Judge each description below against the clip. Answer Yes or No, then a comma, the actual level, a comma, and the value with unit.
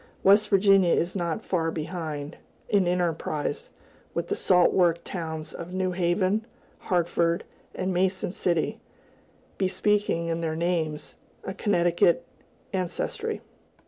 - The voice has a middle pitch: Yes, medium, 175 Hz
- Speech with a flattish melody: Yes, narrow, 2.2 semitones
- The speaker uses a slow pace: Yes, slow, 115 wpm